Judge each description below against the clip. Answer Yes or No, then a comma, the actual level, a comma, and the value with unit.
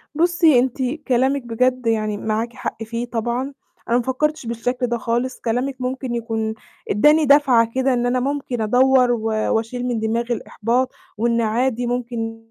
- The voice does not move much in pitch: Yes, narrow, 2.2 semitones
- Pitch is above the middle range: Yes, high, 245 Hz